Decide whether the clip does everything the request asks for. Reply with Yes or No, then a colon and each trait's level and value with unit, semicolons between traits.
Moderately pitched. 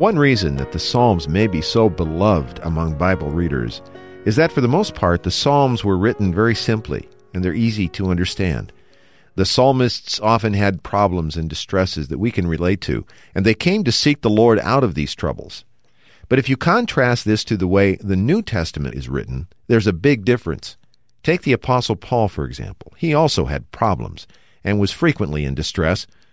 No: low, 100 Hz